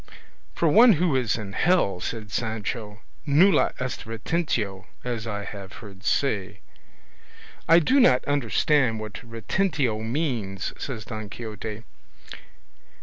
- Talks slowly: Yes, slow, 120 wpm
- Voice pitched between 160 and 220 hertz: No, low, 115 Hz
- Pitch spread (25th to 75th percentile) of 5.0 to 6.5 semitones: Yes, average, 5.3 semitones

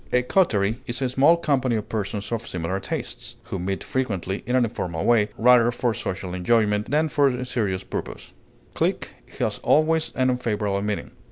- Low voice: Yes, low, 115 Hz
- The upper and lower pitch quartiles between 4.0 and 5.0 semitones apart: Yes, average, 4.5 semitones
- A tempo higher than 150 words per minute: Yes, average, 175 wpm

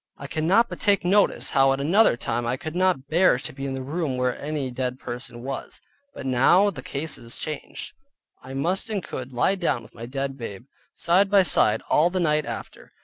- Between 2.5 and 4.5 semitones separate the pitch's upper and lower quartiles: No, wide, 5.5 semitones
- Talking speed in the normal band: No, fast, 210 wpm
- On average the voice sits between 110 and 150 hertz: Yes, medium, 140 Hz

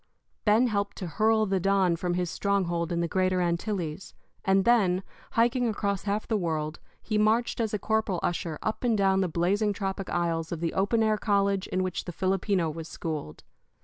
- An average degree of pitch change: Yes, average, 3.5 semitones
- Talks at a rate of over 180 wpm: Yes, average, 190 wpm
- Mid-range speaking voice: No, high, 195 Hz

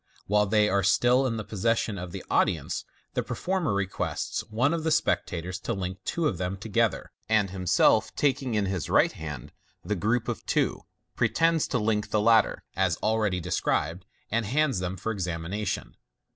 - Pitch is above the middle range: No, low, 105 Hz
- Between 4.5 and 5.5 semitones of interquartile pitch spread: No, average, 3.9 semitones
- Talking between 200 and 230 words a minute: No, average, 175 wpm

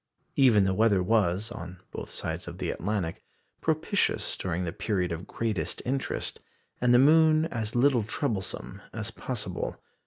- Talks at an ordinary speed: Yes, average, 150 wpm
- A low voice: Yes, low, 110 Hz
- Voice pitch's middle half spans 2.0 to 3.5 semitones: No, average, 4.9 semitones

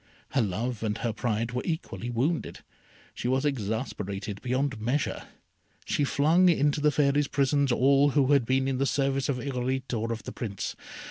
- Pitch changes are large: No, average, 3.5 semitones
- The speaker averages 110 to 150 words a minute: No, average, 175 wpm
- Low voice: Yes, low, 130 Hz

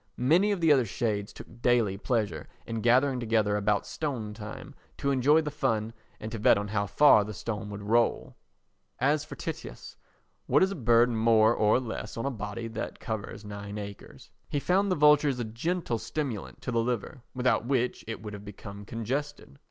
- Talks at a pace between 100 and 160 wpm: No, average, 185 wpm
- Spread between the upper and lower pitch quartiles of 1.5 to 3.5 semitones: No, average, 4.5 semitones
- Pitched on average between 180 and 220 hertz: No, low, 115 Hz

